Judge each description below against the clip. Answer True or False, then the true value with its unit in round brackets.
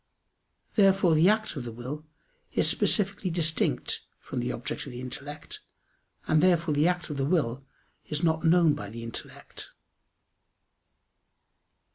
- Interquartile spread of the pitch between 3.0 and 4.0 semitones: False (4.4 semitones)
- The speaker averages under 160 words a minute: True (140 wpm)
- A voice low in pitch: False (155 Hz)